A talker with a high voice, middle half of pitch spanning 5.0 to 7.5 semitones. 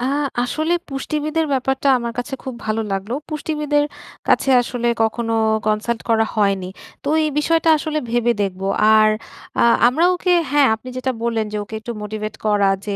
Yes: high, 240 Hz; average, 5.3 semitones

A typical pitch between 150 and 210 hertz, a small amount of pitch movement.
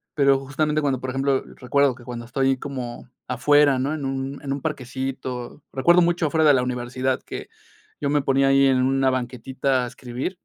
No: low, 135 Hz; narrow, 1.7 semitones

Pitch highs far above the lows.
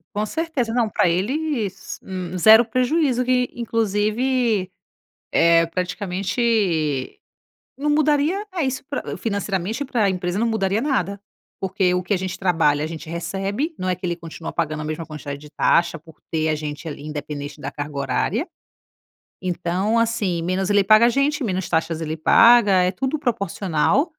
Yes: wide, 6.0 semitones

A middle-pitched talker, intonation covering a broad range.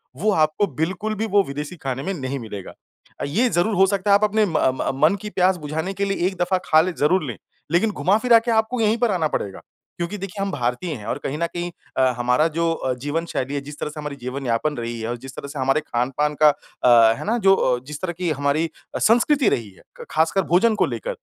Yes: medium, 165 Hz; wide, 6.5 semitones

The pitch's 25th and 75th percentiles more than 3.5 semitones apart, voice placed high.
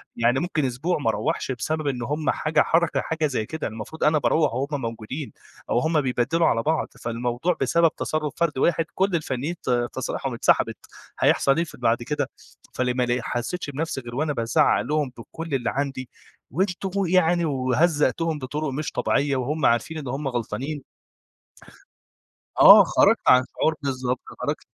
No: average, 4.3 semitones; medium, 140 Hz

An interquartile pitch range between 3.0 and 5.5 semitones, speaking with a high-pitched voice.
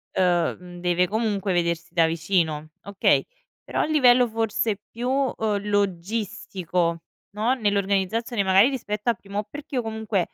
Yes: average, 3.9 semitones; high, 200 Hz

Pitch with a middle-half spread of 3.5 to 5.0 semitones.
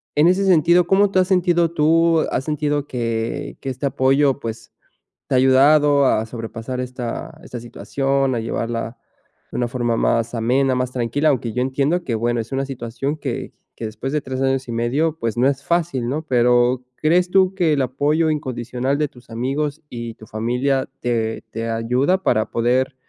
Yes: average, 4.1 semitones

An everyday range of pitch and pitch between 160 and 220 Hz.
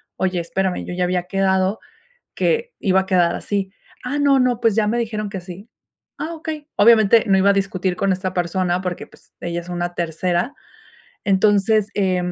Yes: average, 3.2 semitones; high, 190 Hz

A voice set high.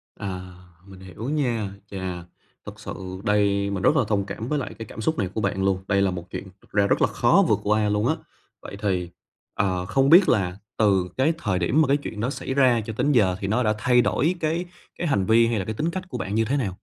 No: low, 105 Hz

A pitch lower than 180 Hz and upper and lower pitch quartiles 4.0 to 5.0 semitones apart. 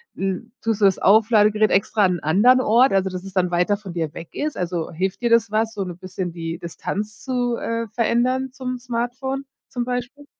No: high, 215 Hz; average, 4.7 semitones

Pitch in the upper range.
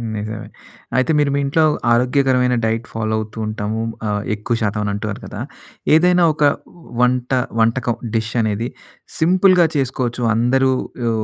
No: low, 120 Hz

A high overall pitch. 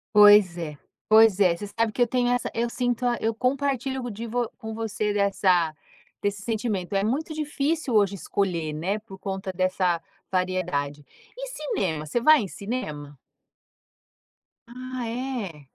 Yes: high, 210 Hz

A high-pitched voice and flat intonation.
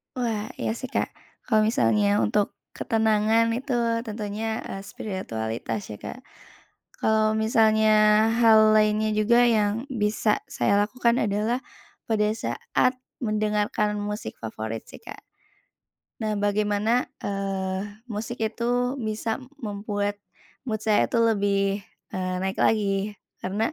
Yes: high, 215 Hz; narrow, 1.7 semitones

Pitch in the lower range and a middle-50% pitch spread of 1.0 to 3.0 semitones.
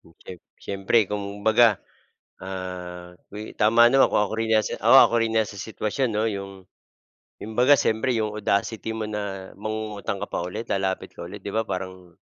Yes: low, 105 Hz; narrow, 2.5 semitones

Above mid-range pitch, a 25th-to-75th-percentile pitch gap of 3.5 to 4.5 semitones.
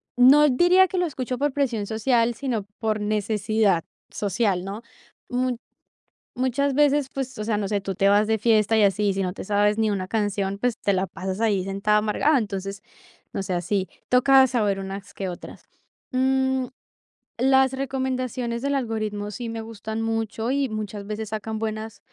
Yes: high, 220 Hz; average, 4.0 semitones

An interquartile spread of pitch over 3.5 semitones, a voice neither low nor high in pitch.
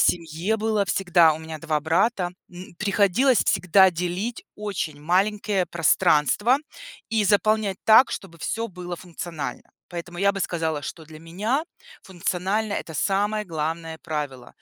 Yes: average, 4.1 semitones; medium, 180 Hz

